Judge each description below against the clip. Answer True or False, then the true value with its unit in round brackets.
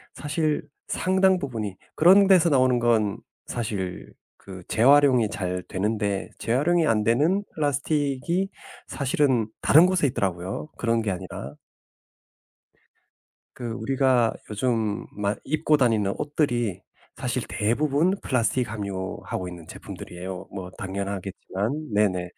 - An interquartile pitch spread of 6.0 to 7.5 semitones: True (6.4 semitones)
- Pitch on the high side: False (115 Hz)